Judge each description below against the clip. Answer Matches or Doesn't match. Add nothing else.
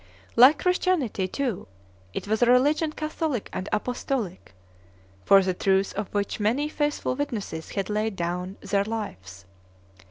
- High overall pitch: Matches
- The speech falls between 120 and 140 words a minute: Matches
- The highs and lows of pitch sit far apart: Matches